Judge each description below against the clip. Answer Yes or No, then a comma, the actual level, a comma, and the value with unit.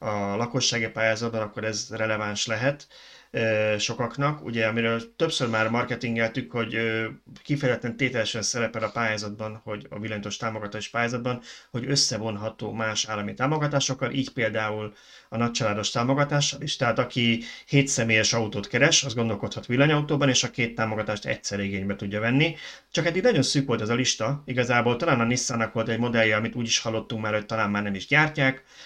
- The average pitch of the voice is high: No, low, 115 Hz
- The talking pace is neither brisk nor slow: No, fast, 160 wpm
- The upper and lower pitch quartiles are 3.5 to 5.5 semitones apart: No, average, 3.1 semitones